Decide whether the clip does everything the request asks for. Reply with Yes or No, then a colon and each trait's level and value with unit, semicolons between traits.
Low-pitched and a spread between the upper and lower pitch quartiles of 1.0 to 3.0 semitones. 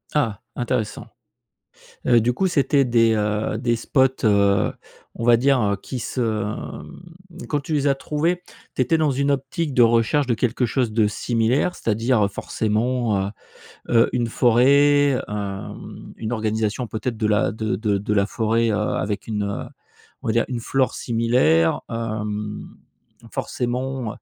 No: low, 115 Hz; average, 3.6 semitones